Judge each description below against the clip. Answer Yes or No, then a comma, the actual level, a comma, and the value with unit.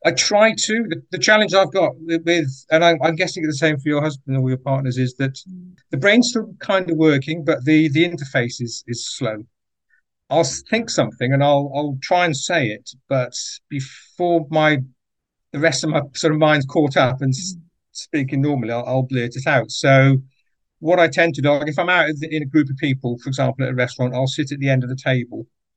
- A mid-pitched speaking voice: Yes, medium, 145 Hz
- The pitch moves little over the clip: No, average, 4.1 semitones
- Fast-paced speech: Yes, fast, 215 wpm